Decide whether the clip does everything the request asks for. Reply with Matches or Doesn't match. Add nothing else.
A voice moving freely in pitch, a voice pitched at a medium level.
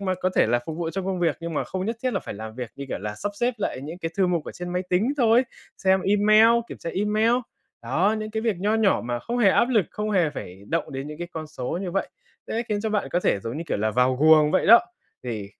Matches